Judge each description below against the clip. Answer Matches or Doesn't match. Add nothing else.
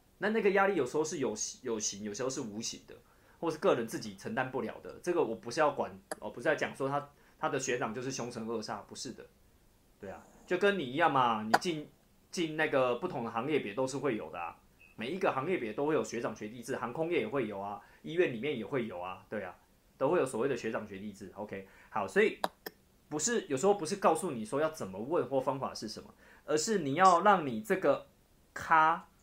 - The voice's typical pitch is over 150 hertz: Doesn't match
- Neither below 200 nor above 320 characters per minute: Doesn't match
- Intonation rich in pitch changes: Matches